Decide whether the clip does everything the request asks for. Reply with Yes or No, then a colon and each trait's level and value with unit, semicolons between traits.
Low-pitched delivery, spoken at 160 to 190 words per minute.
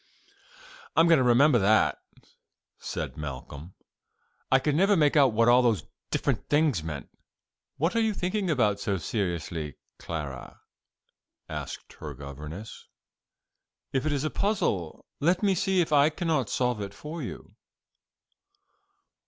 No: low, 125 Hz; average, 140 wpm